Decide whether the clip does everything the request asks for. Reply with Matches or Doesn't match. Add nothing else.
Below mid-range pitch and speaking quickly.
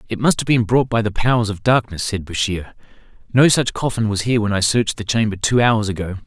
Matches